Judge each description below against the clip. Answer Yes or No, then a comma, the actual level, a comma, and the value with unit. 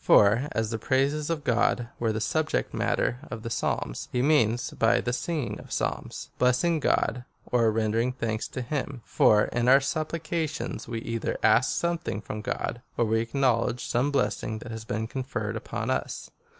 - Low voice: Yes, low, 120 Hz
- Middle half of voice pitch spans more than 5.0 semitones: No, average, 3.6 semitones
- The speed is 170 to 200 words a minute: Yes, average, 185 wpm